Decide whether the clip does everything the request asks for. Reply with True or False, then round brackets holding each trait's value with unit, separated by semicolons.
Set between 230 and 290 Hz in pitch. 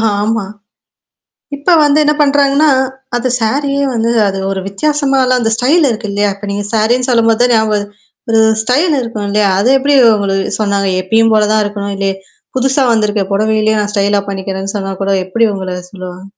False (220 Hz)